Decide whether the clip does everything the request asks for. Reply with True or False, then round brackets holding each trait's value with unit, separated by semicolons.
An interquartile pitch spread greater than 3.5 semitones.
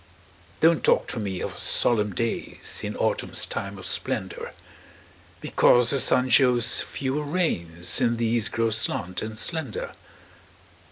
True (3.9 semitones)